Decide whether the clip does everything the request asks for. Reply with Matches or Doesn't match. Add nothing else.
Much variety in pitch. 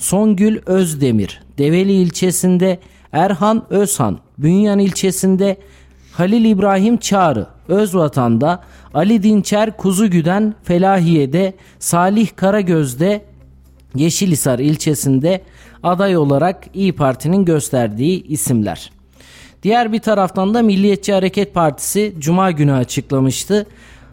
Matches